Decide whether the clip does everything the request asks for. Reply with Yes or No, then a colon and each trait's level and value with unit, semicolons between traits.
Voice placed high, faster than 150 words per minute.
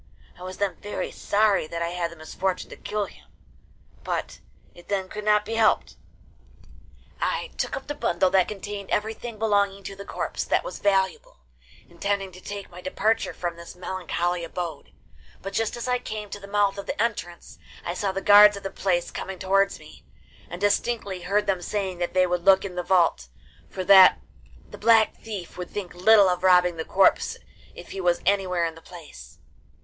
Yes: high, 195 Hz; average, 195 wpm